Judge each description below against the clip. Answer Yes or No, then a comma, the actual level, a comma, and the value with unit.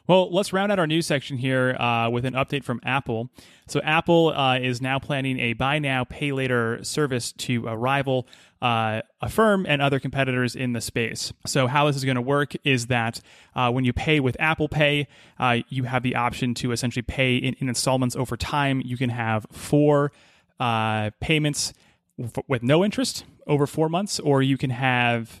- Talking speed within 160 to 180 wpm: No, average, 200 wpm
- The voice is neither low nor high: No, low, 130 Hz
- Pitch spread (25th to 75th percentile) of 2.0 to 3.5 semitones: Yes, average, 3.1 semitones